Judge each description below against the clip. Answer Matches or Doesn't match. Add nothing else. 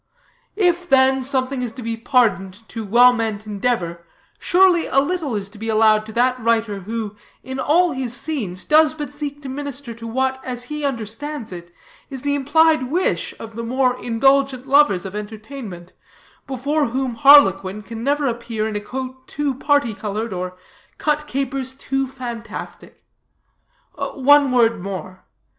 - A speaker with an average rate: Matches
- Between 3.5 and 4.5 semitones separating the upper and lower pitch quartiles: Matches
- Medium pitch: Doesn't match